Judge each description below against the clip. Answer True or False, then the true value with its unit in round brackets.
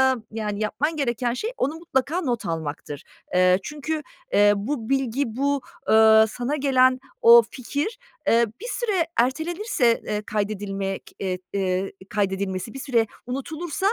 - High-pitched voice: True (240 Hz)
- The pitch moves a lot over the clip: True (5.7 semitones)